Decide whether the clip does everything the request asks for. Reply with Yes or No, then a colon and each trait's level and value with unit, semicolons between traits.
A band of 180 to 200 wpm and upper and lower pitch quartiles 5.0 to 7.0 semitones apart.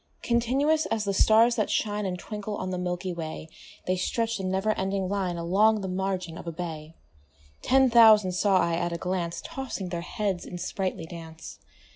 No: average, 185 wpm; average, 3.5 semitones